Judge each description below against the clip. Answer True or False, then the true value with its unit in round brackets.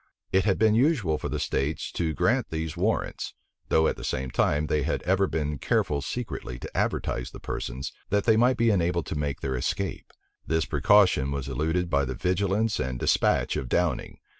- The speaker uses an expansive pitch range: True (6.1 semitones)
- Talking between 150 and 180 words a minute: False (190 wpm)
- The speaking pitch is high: False (80 Hz)